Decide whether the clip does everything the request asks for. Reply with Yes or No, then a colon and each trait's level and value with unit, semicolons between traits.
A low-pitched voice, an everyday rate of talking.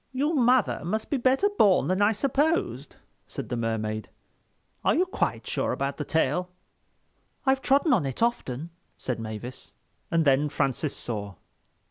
No: medium, 165 Hz; average, 145 wpm